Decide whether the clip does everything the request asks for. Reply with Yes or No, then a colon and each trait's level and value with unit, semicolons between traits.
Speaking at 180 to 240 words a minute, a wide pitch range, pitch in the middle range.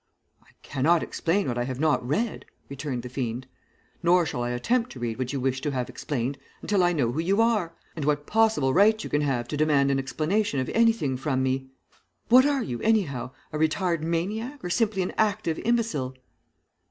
Yes: average, 200 wpm; wide, 7.6 semitones; medium, 155 Hz